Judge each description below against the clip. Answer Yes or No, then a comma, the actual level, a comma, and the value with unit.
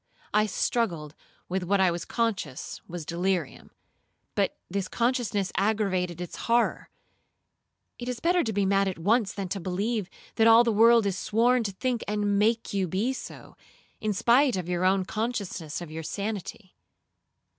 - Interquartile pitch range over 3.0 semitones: Yes, average, 3.9 semitones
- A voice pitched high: Yes, high, 200 Hz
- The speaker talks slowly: No, average, 160 wpm